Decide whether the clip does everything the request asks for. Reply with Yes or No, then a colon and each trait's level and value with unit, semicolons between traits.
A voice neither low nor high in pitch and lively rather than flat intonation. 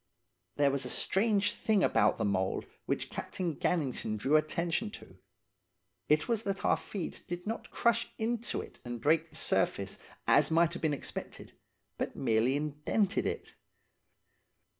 Yes: medium, 165 Hz; wide, 6.5 semitones